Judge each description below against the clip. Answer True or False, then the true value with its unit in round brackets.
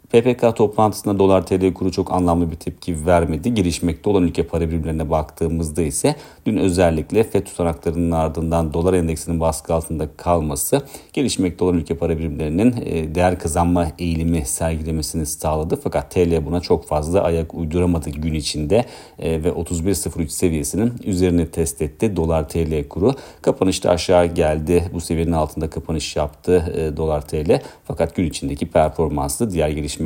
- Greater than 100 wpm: True (140 wpm)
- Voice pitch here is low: True (85 Hz)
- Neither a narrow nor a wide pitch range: False (2.0 semitones)